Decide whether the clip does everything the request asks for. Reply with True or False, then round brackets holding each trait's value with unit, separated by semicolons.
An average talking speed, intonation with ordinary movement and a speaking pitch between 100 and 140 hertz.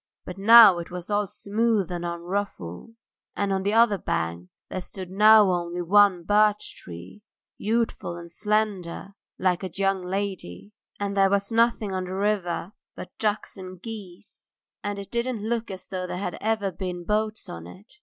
False (170 wpm; 3.0 semitones; 195 Hz)